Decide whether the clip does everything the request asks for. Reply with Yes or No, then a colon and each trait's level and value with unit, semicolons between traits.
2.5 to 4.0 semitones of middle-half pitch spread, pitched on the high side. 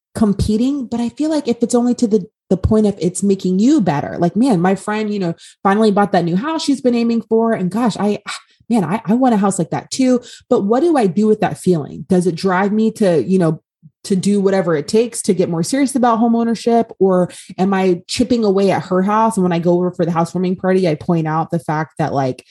No: average, 4.4 semitones; high, 200 Hz